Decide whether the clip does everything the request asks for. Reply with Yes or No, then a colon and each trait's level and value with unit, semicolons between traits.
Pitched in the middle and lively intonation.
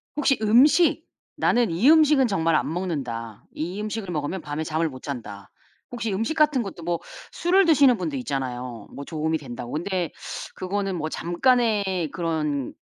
Yes: medium, 175 Hz; wide, 7.5 semitones